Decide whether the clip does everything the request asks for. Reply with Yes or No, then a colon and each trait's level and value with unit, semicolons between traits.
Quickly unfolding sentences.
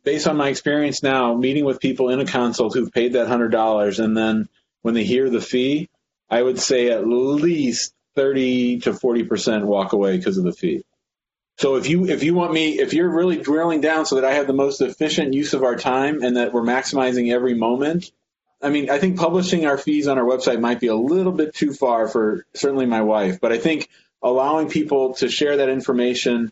Yes: fast, 215 wpm